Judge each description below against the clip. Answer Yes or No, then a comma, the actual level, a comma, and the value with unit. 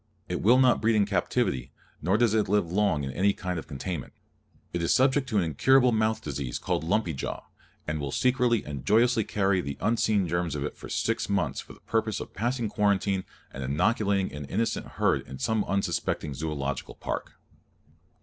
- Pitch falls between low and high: No, low, 100 Hz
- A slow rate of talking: No, average, 190 wpm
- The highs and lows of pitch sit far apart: Yes, wide, 6.4 semitones